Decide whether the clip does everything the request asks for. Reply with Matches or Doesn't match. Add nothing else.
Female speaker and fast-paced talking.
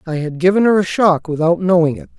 Doesn't match